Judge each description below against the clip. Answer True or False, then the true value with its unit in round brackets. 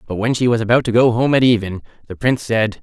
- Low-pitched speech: True (115 Hz)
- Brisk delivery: True (275 wpm)